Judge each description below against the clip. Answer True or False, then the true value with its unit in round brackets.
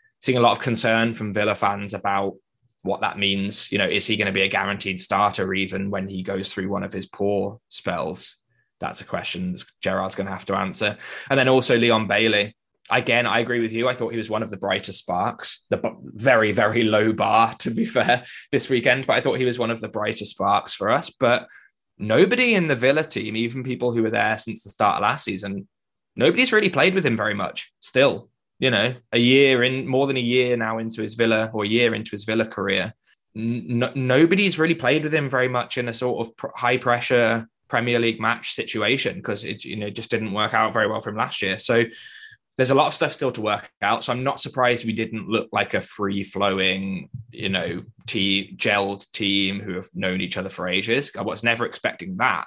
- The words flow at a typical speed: False (230 wpm)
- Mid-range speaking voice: False (115 Hz)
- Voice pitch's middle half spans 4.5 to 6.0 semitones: False (3.5 semitones)